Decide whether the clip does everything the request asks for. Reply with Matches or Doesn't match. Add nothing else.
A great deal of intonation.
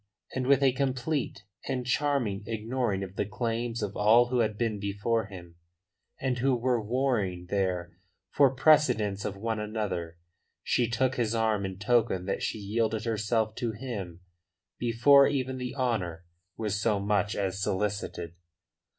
Doesn't match